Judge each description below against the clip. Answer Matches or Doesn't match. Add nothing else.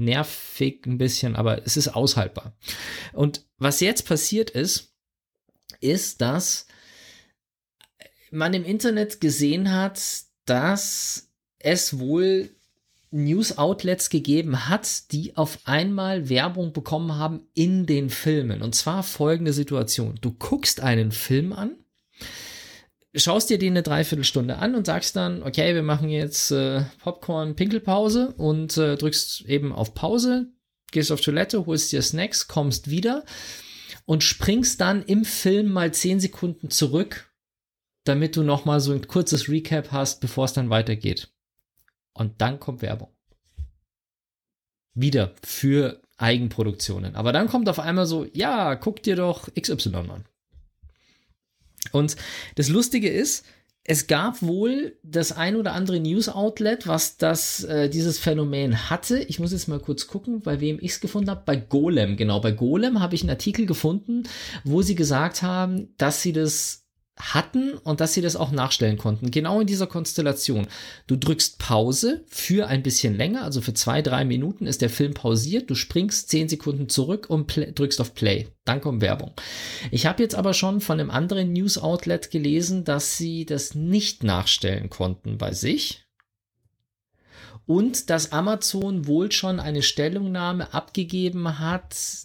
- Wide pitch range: Matches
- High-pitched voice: Doesn't match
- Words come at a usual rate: Matches